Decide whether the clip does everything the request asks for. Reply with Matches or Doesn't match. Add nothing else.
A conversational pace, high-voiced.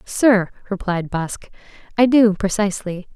Doesn't match